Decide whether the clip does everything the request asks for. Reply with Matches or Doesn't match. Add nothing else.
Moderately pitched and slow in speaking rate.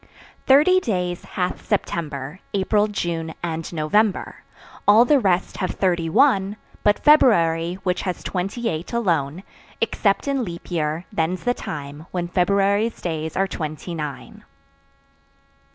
Matches